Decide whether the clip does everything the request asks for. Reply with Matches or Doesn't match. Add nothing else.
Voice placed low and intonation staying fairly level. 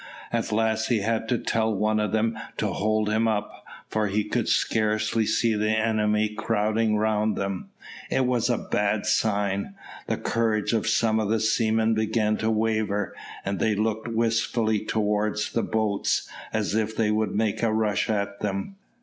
Matches